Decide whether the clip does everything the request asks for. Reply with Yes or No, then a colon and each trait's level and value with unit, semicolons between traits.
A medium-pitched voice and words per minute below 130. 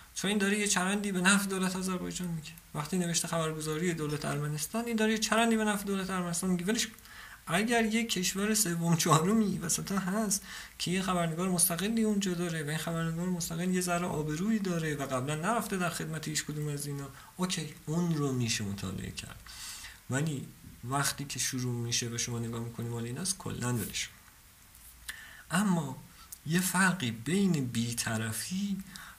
No: medium, 170 Hz; fast, 155 wpm